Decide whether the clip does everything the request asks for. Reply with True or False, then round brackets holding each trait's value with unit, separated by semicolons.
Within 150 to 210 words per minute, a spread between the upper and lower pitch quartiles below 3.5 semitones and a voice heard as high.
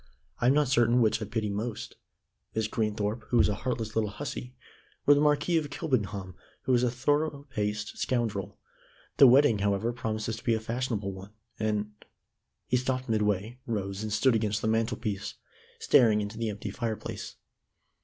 False (175 wpm; 3.0 semitones; 110 Hz)